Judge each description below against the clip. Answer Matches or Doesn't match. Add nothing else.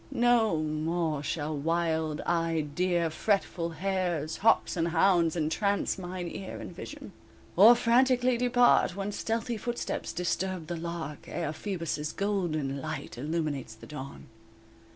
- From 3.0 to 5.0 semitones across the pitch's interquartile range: Matches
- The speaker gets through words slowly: Matches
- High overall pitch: Doesn't match